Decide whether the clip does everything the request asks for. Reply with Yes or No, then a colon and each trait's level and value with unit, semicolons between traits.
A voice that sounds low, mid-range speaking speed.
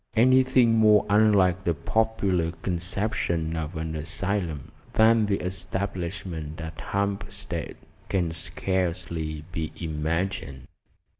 No: very low, 90 Hz; slow, 95 wpm